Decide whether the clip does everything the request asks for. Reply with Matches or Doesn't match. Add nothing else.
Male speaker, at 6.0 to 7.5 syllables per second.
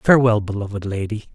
Matches